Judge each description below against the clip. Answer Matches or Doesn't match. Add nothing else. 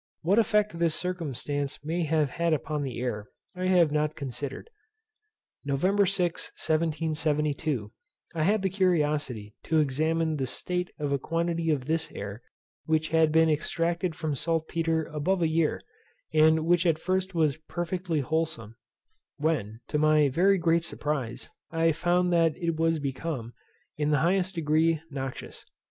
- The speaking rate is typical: Matches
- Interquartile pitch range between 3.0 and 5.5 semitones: Doesn't match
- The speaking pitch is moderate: Matches